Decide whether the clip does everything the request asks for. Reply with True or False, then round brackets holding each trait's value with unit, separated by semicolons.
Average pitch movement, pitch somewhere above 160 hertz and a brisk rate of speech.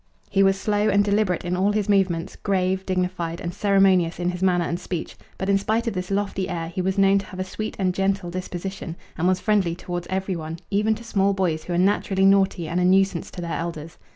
False (2.0 semitones; 190 Hz; 235 wpm)